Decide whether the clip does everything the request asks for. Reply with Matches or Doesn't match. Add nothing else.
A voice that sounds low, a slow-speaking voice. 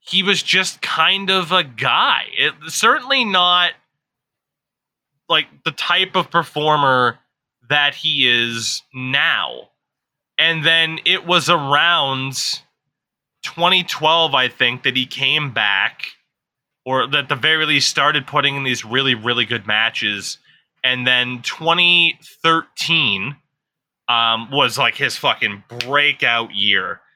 Doesn't match